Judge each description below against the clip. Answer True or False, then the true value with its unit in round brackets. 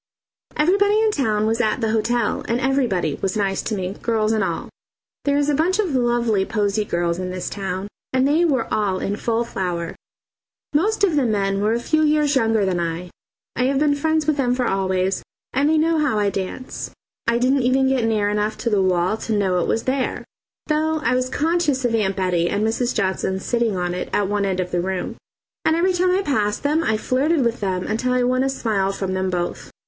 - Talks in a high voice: True (225 Hz)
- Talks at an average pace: False (220 wpm)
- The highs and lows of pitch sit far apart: True (6.1 semitones)